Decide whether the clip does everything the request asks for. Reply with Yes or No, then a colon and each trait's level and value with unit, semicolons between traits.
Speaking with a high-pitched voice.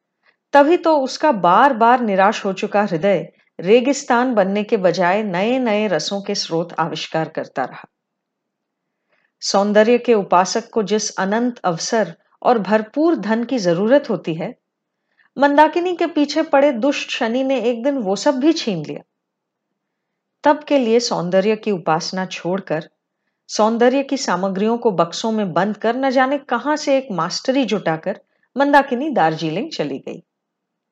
Yes: high, 220 Hz